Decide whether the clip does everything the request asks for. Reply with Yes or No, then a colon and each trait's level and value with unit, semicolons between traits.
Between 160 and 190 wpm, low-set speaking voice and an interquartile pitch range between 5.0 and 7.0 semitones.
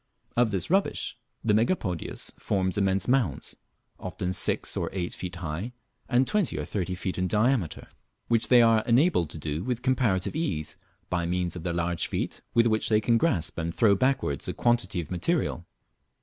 Yes: average, 180 wpm; low, 100 Hz; wide, 5.5 semitones